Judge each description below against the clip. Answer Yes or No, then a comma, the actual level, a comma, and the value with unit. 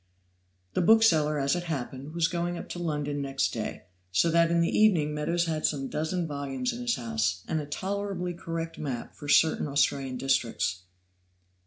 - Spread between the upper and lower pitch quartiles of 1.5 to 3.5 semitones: No, average, 3.9 semitones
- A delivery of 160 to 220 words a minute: Yes, average, 175 wpm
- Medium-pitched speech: Yes, medium, 155 Hz